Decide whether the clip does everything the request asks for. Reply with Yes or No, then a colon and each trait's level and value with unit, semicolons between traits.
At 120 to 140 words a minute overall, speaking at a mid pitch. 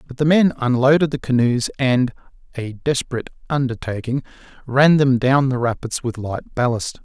No: slow, 135 wpm; low, 130 Hz